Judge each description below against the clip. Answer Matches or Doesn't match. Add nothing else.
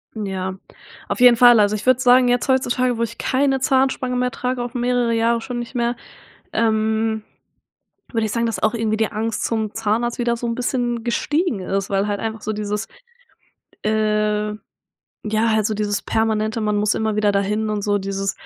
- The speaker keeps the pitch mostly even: Matches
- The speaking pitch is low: Doesn't match